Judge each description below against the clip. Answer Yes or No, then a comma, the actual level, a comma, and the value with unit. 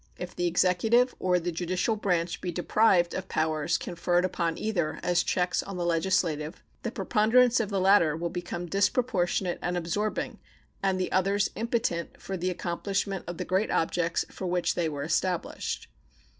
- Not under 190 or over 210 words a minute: No, average, 165 wpm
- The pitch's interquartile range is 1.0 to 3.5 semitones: Yes, narrow, 2.4 semitones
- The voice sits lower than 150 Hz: No, medium, 180 Hz